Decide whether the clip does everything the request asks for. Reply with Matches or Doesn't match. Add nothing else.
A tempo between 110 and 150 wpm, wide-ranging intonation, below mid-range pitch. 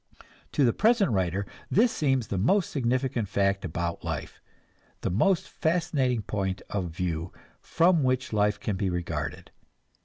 Matches